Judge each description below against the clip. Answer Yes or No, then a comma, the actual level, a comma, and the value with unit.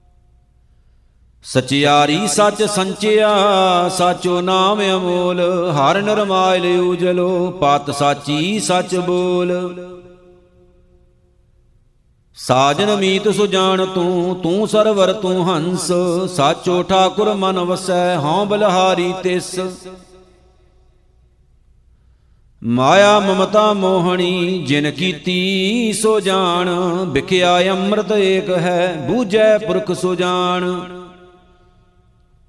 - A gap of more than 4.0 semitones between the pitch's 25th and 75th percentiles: No, average, 2.8 semitones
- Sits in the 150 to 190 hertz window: Yes, medium, 180 Hz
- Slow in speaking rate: Yes, slow, 80 wpm